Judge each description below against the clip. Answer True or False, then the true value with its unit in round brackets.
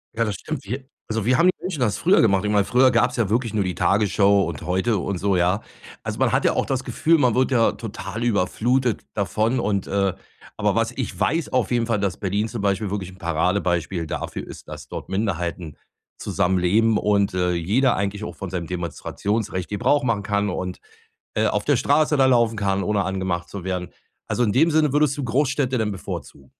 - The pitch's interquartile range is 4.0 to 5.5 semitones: True (4.4 semitones)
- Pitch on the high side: False (105 Hz)